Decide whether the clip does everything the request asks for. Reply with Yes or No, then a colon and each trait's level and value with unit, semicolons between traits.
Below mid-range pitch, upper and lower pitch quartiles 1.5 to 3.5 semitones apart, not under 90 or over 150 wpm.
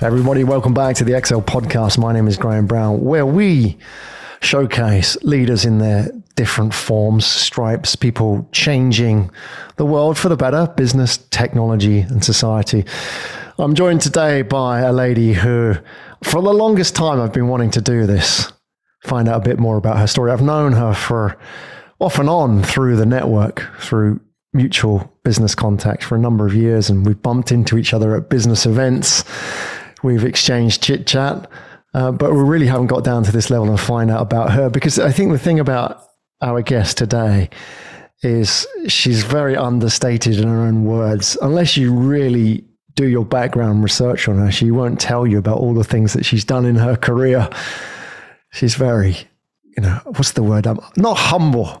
No: low, 120 Hz; average, 3.0 semitones; average, 175 wpm